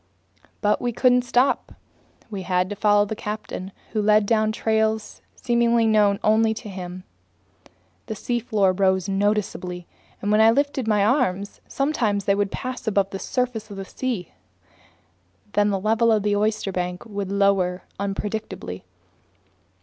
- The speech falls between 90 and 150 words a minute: Yes, average, 145 wpm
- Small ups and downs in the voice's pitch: Yes, narrow, 2.3 semitones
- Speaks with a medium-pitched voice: No, high, 210 Hz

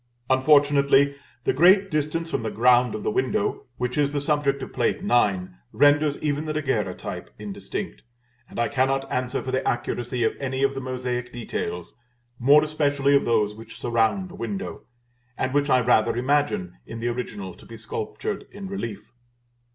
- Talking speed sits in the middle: Yes, average, 170 wpm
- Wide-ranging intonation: No, average, 3.7 semitones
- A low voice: Yes, low, 130 Hz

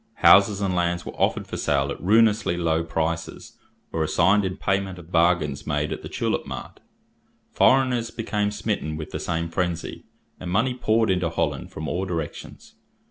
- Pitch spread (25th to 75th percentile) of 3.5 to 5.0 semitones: Yes, average, 3.9 semitones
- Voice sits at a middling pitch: No, very low, 90 Hz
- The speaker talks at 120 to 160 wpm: No, average, 170 wpm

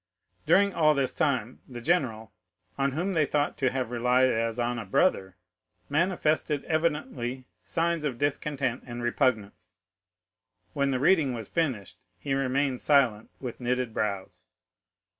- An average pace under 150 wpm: Yes, average, 140 wpm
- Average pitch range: Yes, average, 4.0 semitones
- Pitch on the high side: No, low, 130 Hz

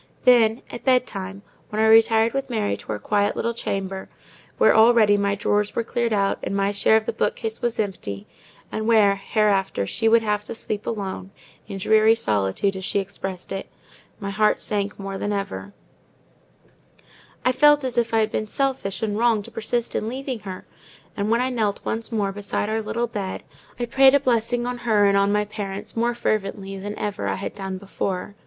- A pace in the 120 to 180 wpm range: No, average, 195 wpm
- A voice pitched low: No, high, 210 Hz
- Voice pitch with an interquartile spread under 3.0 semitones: Yes, narrow, 2.6 semitones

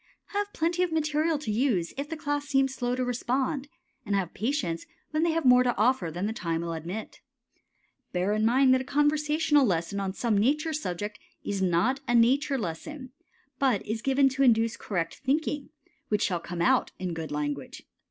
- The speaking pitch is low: No, very high, 250 Hz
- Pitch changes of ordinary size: No, wide, 7.1 semitones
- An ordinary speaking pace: Yes, average, 190 wpm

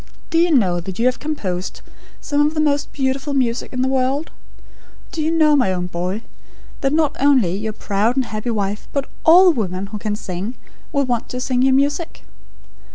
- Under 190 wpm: No, average, 195 wpm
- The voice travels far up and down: Yes, wide, 5.8 semitones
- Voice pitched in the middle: No, very high, 255 Hz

